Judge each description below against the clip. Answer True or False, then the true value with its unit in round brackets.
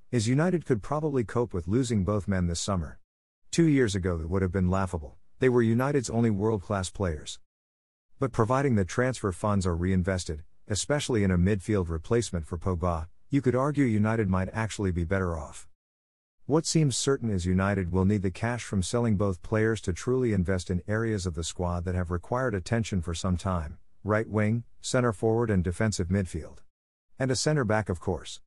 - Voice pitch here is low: True (100 Hz)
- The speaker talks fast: False (190 wpm)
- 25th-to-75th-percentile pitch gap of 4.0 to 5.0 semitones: True (4.5 semitones)